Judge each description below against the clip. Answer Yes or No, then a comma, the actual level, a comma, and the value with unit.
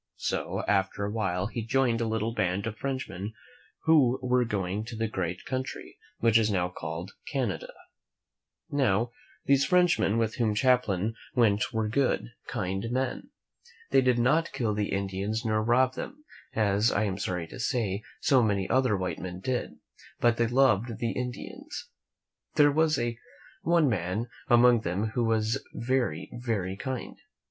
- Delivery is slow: No, average, 155 wpm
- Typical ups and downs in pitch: Yes, average, 4.1 semitones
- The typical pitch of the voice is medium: No, low, 115 Hz